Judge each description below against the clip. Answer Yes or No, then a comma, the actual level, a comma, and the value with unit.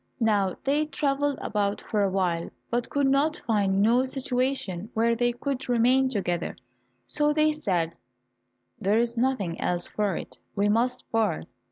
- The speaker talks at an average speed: Yes, average, 150 wpm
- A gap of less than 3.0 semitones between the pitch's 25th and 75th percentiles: No, average, 5.0 semitones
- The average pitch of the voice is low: No, high, 230 Hz